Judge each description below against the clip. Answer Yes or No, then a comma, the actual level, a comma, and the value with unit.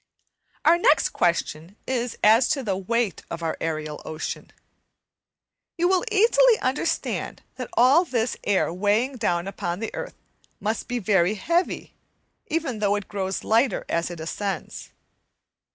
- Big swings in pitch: Yes, wide, 6.3 semitones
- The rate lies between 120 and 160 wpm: Yes, average, 140 wpm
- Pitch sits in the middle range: No, high, 215 Hz